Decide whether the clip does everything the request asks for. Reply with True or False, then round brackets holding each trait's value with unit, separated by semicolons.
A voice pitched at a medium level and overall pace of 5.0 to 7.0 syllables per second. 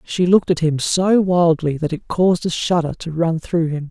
True (170 Hz; 5.1 syllables/s)